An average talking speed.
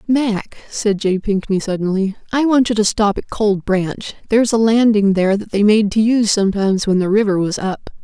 No: fast, 210 wpm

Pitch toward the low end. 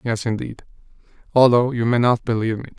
Yes: low, 120 Hz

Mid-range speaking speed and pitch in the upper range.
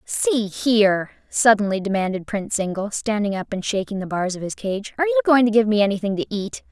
No: fast, 215 wpm; high, 210 Hz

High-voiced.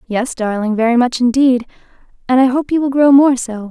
Yes: very high, 250 Hz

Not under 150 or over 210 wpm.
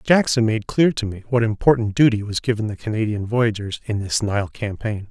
Yes: average, 200 wpm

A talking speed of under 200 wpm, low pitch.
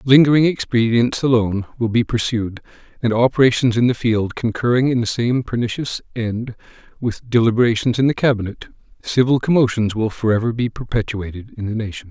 Yes: average, 155 wpm; low, 115 Hz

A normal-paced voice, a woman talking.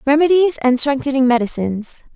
No: slow, 110 wpm; female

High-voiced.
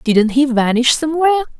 Yes: very high, 270 Hz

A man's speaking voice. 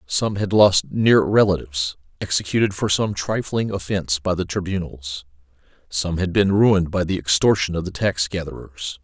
Yes: male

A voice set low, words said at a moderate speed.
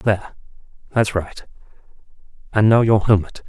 No: low, 105 Hz; slow, 120 wpm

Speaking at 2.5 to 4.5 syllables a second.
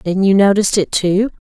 No: 5.8 syllables/s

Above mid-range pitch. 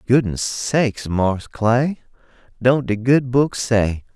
No: low, 120 Hz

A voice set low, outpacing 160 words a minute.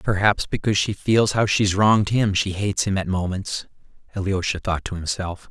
Yes: low, 100 Hz; average, 185 wpm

